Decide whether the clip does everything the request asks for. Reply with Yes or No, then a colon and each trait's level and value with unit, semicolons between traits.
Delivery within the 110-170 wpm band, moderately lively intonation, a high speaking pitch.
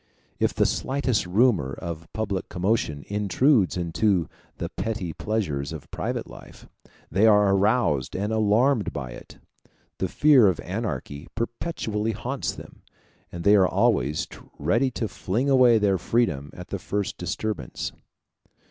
No: average, 140 wpm; average, 4.7 semitones; low, 105 Hz